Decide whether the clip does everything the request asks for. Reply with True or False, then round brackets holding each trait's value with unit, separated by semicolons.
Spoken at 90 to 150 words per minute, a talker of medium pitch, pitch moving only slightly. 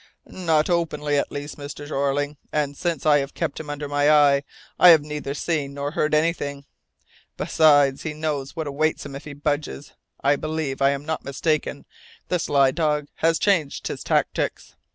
False (175 wpm; 145 Hz; 1.7 semitones)